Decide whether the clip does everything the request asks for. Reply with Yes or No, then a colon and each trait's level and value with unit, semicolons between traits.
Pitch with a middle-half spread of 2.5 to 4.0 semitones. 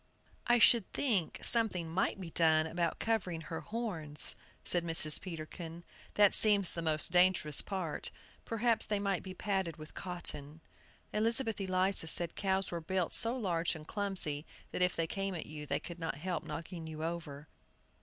Yes: average, 3.5 semitones